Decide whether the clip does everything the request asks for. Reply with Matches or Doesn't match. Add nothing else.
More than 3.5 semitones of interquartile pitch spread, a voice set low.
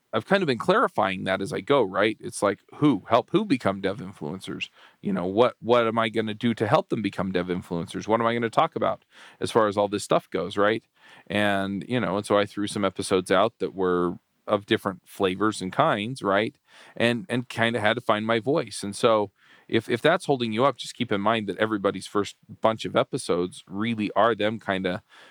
Doesn't match